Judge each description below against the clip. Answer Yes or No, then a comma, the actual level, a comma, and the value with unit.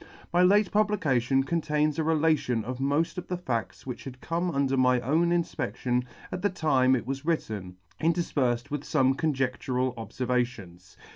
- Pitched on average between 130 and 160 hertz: Yes, low, 135 Hz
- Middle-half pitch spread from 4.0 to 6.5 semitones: Yes, average, 4.6 semitones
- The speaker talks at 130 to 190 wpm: Yes, average, 155 wpm